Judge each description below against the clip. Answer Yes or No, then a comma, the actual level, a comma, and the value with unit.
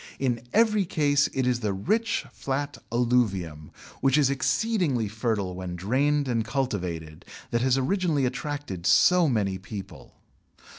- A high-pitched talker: No, low, 125 Hz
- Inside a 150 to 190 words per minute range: No, slow, 135 wpm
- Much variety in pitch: Yes, wide, 6.2 semitones